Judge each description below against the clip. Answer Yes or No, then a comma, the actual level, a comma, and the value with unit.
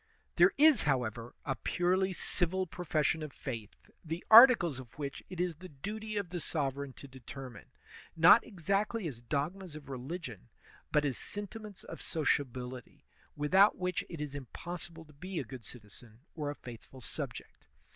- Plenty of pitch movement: Yes, wide, 5.7 semitones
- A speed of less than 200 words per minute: Yes, average, 155 wpm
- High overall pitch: No, medium, 155 Hz